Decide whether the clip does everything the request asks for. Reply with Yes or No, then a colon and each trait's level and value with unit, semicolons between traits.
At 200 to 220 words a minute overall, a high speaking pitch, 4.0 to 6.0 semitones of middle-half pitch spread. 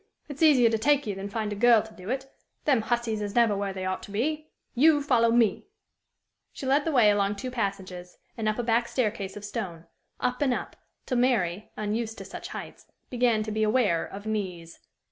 No: fast, 205 wpm; high, 220 Hz; average, 3.6 semitones